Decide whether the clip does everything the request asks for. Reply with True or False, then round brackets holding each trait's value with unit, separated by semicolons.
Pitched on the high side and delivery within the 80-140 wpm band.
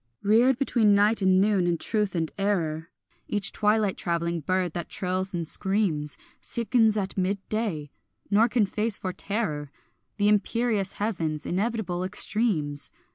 True (195 Hz; 135 wpm)